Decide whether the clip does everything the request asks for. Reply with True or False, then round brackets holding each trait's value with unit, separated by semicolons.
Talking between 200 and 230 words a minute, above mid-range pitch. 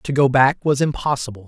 False (205 wpm; 135 Hz)